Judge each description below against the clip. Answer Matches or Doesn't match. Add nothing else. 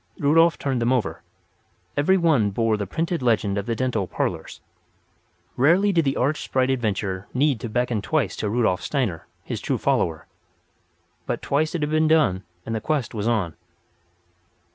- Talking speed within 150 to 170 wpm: Matches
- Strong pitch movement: Matches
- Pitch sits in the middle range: Doesn't match